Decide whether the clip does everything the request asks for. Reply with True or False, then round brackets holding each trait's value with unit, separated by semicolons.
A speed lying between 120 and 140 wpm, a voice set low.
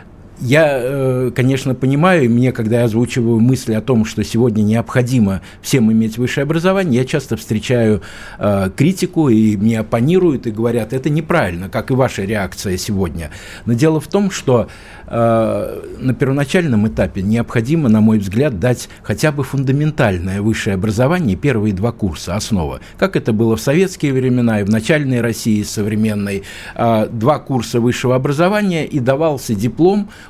False (150 wpm; 120 Hz)